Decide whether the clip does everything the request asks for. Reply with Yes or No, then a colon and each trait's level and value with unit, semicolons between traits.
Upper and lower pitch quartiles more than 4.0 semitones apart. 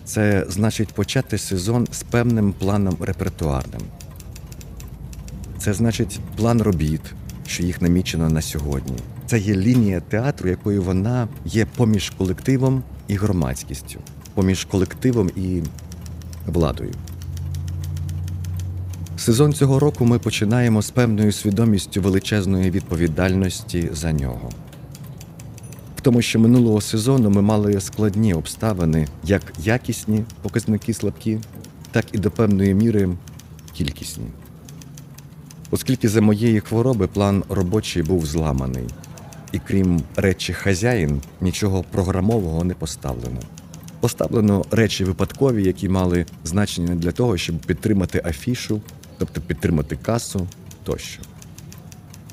Yes: average, 4.4 semitones